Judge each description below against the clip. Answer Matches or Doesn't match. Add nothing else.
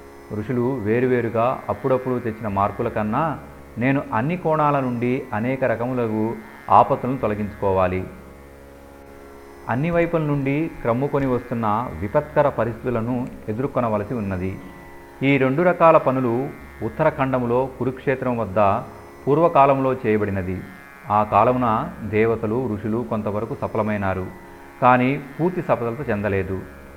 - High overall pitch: Doesn't match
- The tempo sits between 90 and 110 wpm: Matches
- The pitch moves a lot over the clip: Doesn't match